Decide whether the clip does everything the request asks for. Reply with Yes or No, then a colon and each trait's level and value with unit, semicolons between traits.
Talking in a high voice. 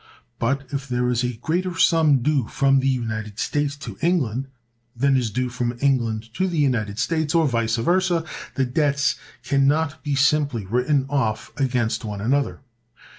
No: low, 135 Hz